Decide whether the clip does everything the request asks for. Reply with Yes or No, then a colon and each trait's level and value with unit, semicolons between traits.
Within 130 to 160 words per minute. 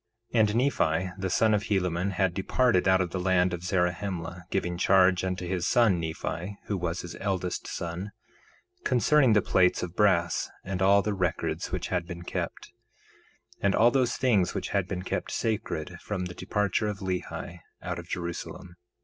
No: average, 175 wpm